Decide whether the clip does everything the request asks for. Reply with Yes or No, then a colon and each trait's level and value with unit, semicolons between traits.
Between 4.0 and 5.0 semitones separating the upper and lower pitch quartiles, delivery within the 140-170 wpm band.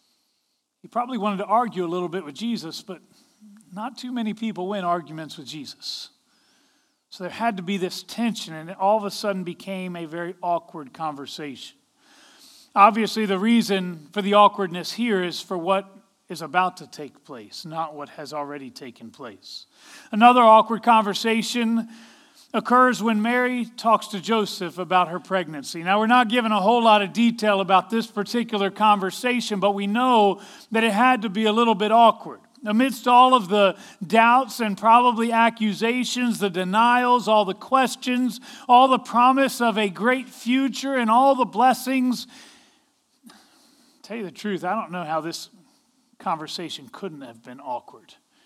Yes: average, 4.6 semitones; average, 165 wpm